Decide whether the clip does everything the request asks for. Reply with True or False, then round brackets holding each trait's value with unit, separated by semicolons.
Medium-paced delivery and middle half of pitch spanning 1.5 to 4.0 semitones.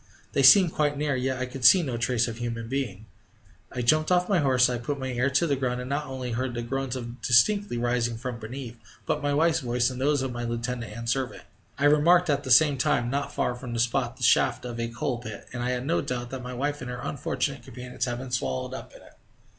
False (255 wpm; 2.6 semitones)